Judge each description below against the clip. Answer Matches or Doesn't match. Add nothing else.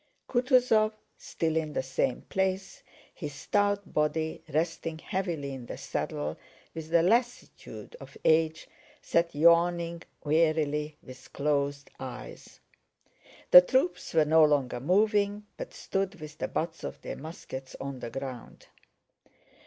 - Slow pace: Matches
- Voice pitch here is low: Doesn't match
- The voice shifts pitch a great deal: Doesn't match